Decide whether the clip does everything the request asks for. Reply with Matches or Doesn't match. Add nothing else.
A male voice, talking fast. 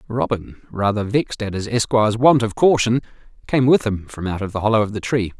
Matches